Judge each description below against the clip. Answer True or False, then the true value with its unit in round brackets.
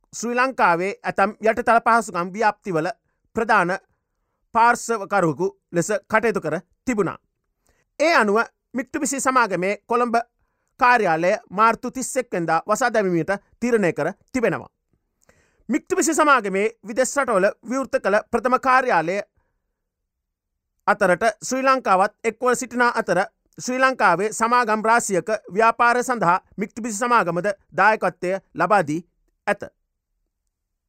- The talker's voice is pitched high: True (220 Hz)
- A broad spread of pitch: False (4.6 semitones)